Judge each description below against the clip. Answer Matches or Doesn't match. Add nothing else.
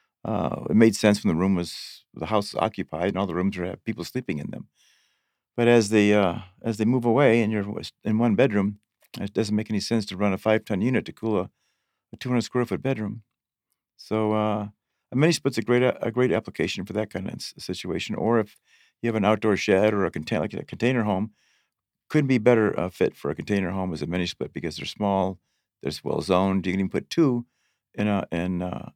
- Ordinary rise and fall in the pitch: Matches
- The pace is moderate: Doesn't match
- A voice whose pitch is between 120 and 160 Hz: Doesn't match